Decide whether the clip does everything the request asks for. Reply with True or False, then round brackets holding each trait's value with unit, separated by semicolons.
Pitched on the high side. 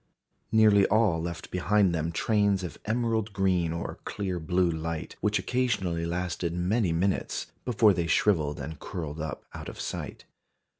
False (90 Hz)